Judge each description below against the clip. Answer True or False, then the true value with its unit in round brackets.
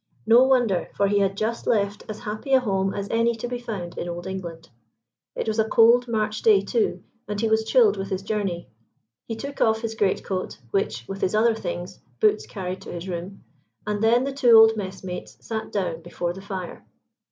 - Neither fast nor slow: False (210 wpm)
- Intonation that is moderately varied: True (3.0 semitones)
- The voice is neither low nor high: False (210 Hz)